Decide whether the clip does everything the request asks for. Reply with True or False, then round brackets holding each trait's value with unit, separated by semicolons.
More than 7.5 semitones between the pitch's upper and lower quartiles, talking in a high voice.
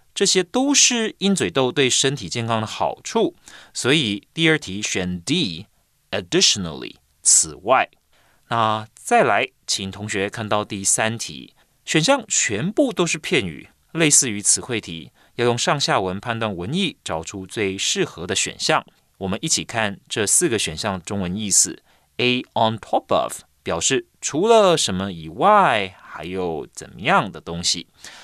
False (7.9 semitones; 110 Hz)